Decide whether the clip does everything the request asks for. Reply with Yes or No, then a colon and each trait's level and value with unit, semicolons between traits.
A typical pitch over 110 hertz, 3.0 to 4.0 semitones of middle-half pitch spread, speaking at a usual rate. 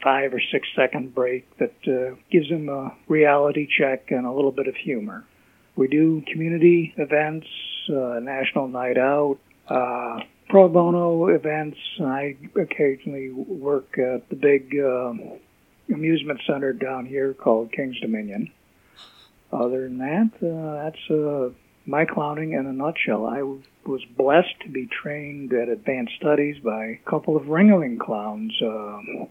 Yes: medium, 140 Hz; average, 3.3 semitones; average, 145 wpm